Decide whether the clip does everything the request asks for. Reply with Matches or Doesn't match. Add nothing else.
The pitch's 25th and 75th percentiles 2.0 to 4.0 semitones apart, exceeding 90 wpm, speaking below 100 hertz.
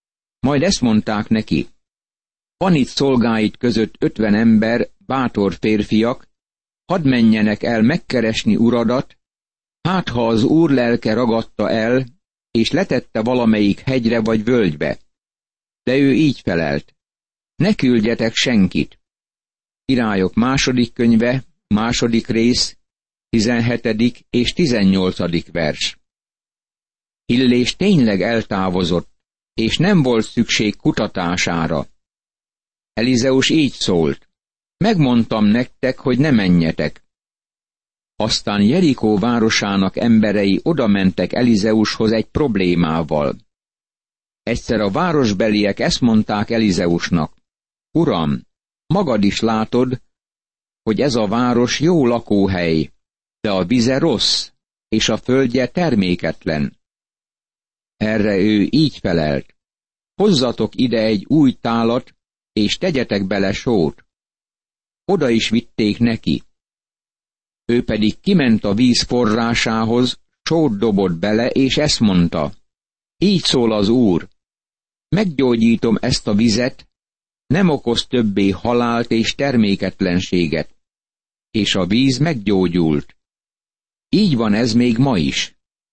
Doesn't match